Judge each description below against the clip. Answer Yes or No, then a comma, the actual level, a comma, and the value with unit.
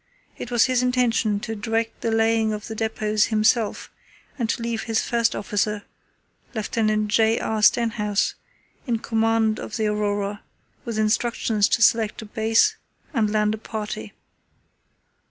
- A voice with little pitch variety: Yes, narrow, 1.3 semitones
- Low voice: No, high, 220 Hz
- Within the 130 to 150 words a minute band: Yes, average, 145 wpm